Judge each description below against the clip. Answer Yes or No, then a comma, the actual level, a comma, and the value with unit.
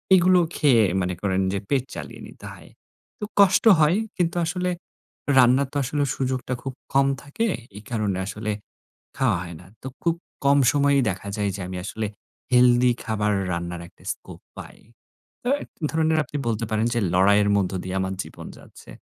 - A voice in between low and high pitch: No, low, 120 Hz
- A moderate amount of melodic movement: No, wide, 5.9 semitones